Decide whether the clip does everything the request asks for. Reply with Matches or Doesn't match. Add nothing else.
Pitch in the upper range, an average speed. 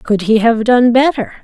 Doesn't match